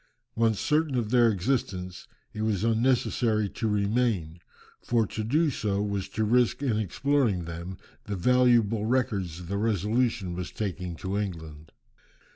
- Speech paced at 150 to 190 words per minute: No, average, 140 wpm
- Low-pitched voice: Yes, low, 105 Hz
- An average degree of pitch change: Yes, average, 4.3 semitones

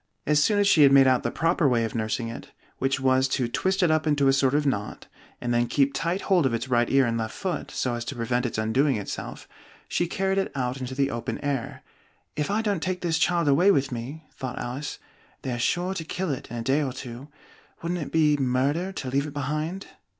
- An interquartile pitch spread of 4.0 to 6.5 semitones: Yes, average, 4.7 semitones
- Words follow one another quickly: Yes, fast, 240 wpm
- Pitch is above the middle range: No, low, 135 Hz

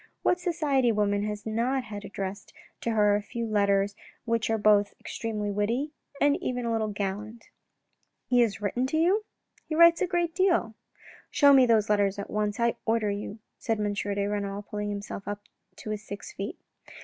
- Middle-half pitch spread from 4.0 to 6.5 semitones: No, average, 3.4 semitones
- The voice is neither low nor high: No, high, 215 Hz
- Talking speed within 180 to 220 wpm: Yes, average, 200 wpm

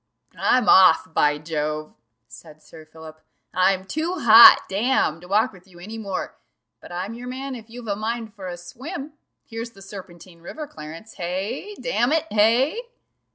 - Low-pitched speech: No, high, 200 Hz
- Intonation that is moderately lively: No, wide, 5.8 semitones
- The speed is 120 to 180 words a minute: Yes, average, 165 wpm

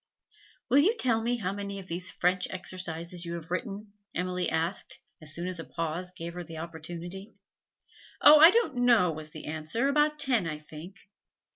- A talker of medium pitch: Yes, medium, 180 Hz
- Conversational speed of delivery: Yes, average, 180 wpm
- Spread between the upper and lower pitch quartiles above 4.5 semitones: Yes, average, 5.1 semitones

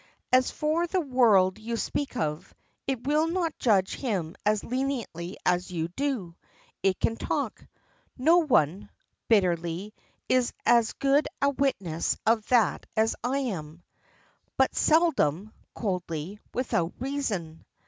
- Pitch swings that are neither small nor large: No, wide, 7.2 semitones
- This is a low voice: No, high, 220 Hz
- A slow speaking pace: Yes, slow, 130 wpm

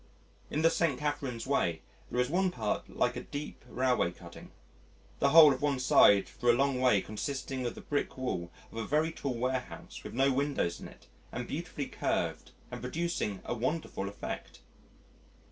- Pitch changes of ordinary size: Yes, average, 3.8 semitones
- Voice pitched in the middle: No, low, 130 Hz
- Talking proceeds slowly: No, average, 175 wpm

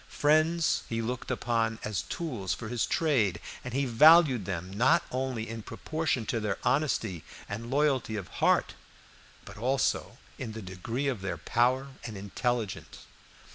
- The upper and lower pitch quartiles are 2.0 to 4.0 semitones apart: No, average, 4.5 semitones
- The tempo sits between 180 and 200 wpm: No, average, 150 wpm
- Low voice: Yes, low, 120 Hz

